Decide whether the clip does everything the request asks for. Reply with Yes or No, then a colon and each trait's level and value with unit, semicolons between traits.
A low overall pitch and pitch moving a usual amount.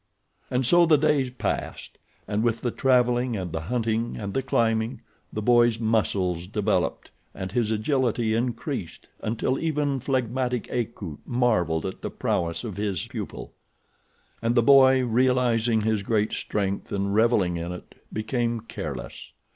Yes: low, 115 Hz; average, 3.4 semitones